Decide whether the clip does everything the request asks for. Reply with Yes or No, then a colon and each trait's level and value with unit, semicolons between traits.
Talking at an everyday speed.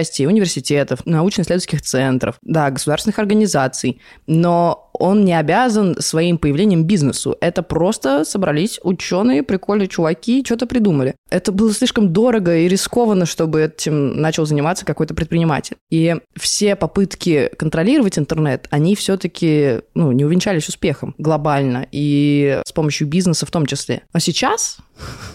Yes: average, 130 wpm